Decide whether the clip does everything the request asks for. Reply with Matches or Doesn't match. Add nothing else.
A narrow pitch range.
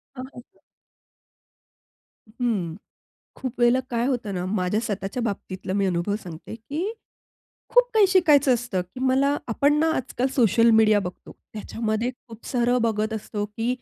Doesn't match